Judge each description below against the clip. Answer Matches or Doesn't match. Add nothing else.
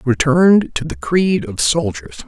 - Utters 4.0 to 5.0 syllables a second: Matches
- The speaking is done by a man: Matches